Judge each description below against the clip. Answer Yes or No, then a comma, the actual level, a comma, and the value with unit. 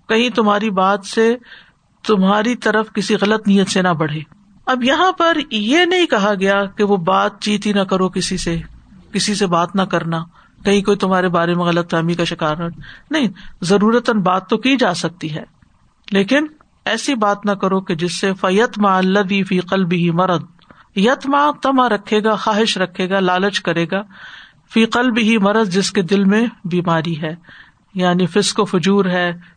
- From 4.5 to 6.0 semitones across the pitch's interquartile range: No, average, 3.3 semitones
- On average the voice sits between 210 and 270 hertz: No, high, 200 Hz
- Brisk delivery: No, average, 180 wpm